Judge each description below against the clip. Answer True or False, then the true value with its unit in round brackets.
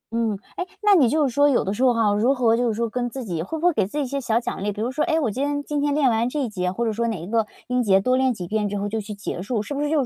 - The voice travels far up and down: False (5.0 semitones)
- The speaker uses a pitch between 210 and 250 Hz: True (235 Hz)